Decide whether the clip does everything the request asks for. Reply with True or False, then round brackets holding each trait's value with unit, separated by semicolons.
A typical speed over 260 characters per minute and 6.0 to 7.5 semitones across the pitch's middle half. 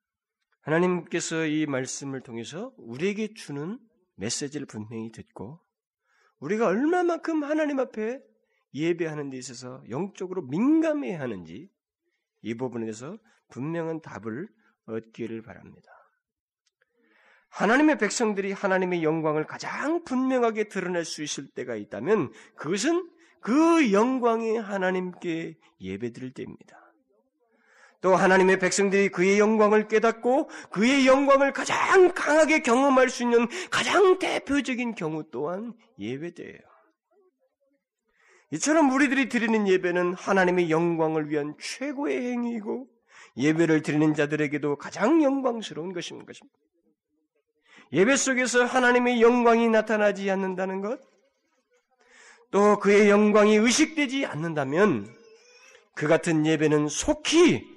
False (280 characters per minute; 8.8 semitones)